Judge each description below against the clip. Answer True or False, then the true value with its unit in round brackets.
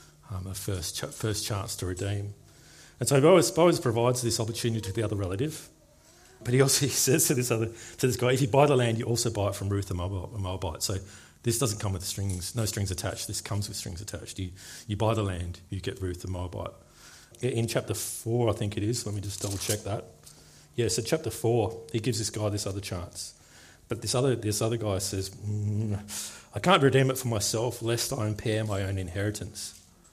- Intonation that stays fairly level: False (3.2 semitones)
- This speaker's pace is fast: True (215 wpm)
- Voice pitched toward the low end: True (105 Hz)